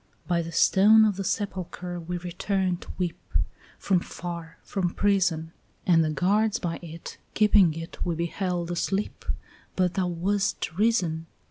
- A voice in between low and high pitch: Yes, medium, 180 Hz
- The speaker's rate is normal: Yes, average, 145 wpm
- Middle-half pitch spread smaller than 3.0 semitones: Yes, narrow, 2.6 semitones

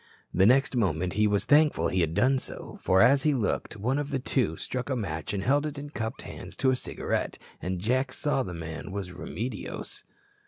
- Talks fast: Yes, fast, 210 wpm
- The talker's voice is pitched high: No, low, 115 Hz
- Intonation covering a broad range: Yes, wide, 6.2 semitones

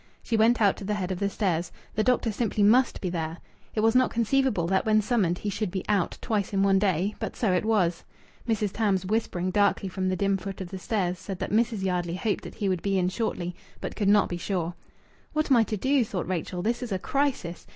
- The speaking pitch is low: No, high, 200 Hz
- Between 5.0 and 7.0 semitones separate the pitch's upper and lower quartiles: No, average, 3.2 semitones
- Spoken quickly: Yes, fast, 245 wpm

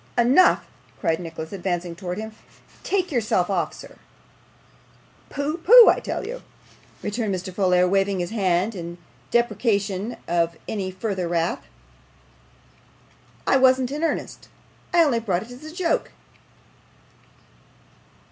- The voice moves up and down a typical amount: No, wide, 6.2 semitones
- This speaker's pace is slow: Yes, slow, 120 wpm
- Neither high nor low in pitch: No, high, 200 Hz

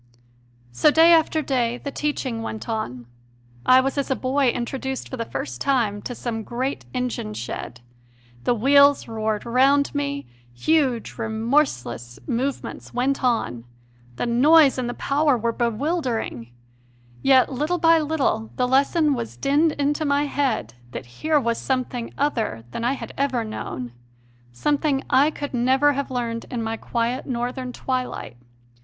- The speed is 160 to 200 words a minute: No, average, 150 wpm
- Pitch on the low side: No, very high, 255 Hz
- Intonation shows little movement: No, average, 3.6 semitones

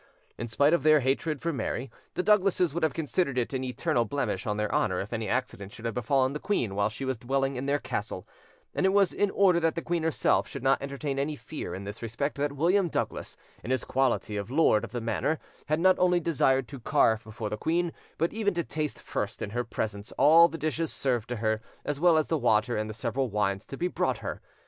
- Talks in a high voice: No, low, 135 Hz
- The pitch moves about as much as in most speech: No, wide, 6.1 semitones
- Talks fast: Yes, fast, 240 wpm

